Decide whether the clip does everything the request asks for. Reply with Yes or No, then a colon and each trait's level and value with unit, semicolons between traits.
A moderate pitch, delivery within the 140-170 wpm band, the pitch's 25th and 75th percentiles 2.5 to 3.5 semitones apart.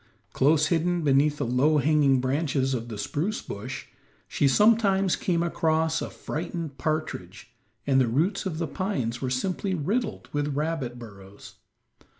No: medium, 150 Hz; average, 150 wpm; average, 4.7 semitones